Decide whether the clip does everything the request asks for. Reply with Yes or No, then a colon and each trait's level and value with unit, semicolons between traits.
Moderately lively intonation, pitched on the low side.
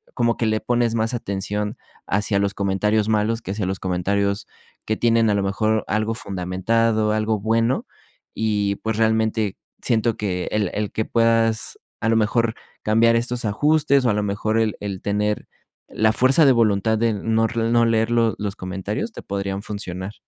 No: narrow, 2.2 semitones; low, 110 Hz